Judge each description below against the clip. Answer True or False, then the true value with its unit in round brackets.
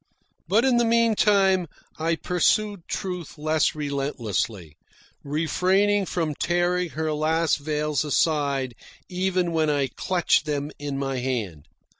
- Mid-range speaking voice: True (160 Hz)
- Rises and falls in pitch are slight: False (4.3 semitones)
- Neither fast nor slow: False (120 wpm)